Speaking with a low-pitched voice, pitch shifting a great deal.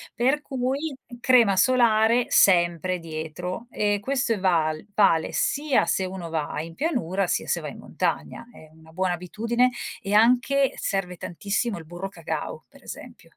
No: high, 195 Hz; wide, 6.1 semitones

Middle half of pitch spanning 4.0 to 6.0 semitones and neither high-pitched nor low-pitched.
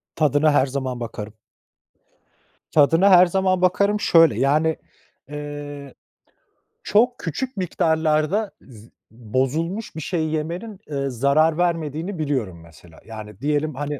Yes: average, 4.3 semitones; medium, 155 Hz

